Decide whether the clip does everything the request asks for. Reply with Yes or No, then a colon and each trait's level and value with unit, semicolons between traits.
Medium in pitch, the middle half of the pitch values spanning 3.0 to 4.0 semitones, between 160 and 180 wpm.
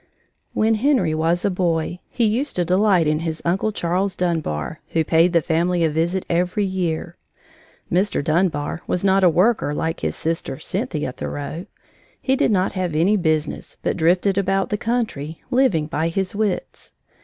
Yes: medium, 175 Hz; average, 3.4 semitones; average, 165 wpm